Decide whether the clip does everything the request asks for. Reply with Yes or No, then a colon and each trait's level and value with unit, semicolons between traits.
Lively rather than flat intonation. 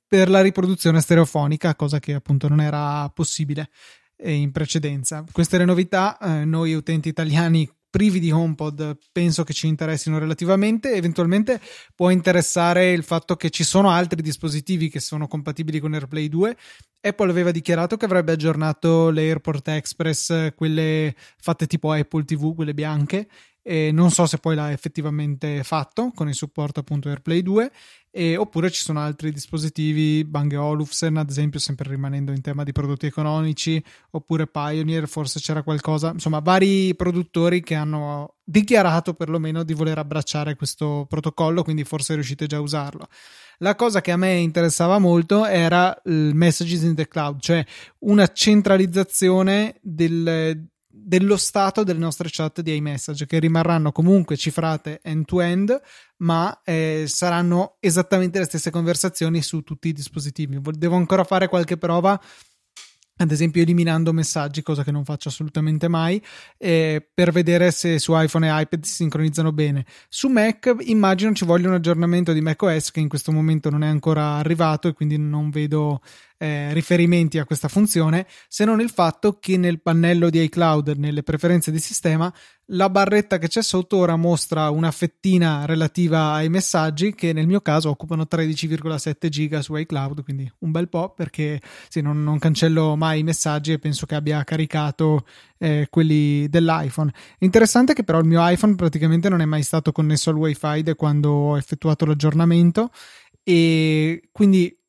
No: narrow, 2.4 semitones